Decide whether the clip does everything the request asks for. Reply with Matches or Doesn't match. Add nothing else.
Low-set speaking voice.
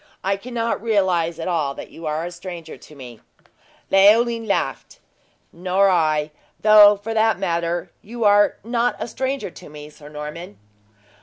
Doesn't match